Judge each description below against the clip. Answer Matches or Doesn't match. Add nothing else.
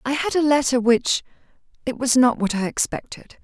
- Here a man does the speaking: Doesn't match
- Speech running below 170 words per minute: Doesn't match